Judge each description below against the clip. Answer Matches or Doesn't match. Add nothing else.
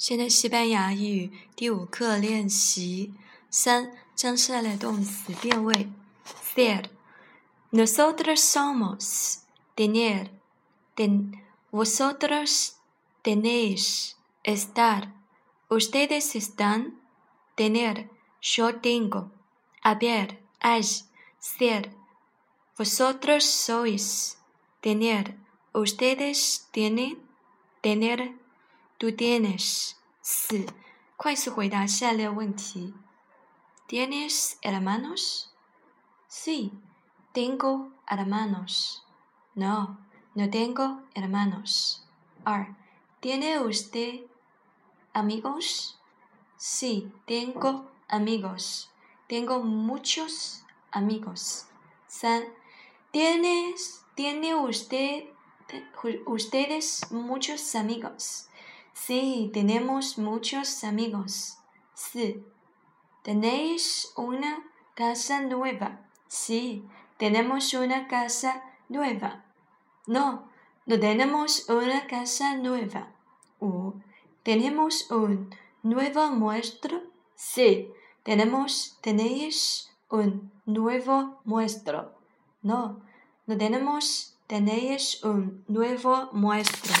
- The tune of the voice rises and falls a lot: Doesn't match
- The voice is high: Matches